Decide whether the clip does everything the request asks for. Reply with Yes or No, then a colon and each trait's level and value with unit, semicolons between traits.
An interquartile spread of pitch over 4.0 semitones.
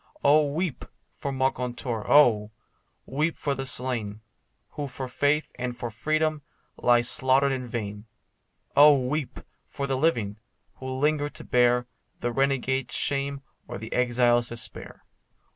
No: average, 2.8 semitones